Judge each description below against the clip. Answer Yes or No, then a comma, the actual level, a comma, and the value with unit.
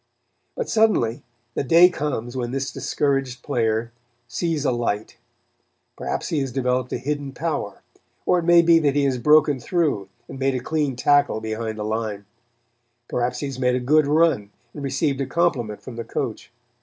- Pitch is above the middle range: No, low, 135 Hz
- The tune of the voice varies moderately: Yes, average, 4.1 semitones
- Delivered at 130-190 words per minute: Yes, average, 180 wpm